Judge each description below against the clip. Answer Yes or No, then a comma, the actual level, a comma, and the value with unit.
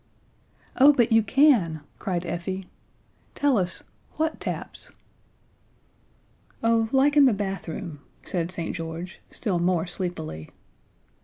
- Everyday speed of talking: No, slow, 110 wpm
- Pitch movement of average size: No, wide, 5.7 semitones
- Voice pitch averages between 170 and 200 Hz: Yes, high, 190 Hz